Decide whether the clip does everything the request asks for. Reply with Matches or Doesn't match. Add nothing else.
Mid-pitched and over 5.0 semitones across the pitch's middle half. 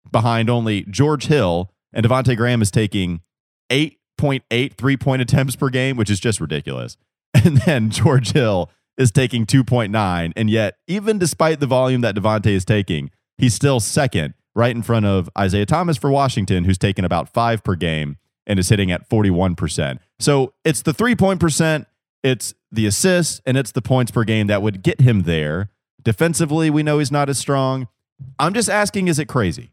Doesn't match